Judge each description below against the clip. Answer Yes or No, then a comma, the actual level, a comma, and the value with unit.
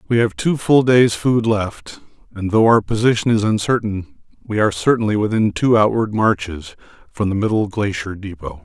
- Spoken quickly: No, average, 175 wpm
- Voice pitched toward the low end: Yes, low, 105 Hz